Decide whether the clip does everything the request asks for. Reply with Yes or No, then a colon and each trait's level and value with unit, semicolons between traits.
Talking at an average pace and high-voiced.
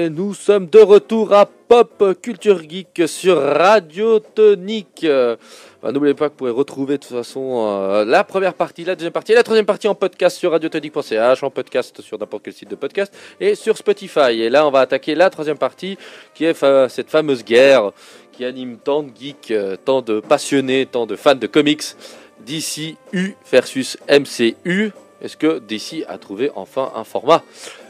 No: average, 175 wpm; medium, 160 Hz